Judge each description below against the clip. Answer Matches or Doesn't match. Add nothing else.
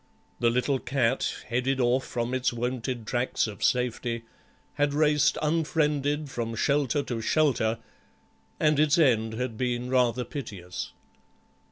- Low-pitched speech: Matches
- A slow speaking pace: Matches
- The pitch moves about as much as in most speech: Matches